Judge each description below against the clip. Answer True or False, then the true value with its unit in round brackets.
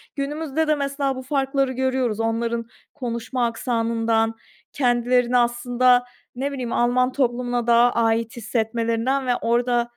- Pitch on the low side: False (245 Hz)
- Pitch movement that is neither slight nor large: False (2.0 semitones)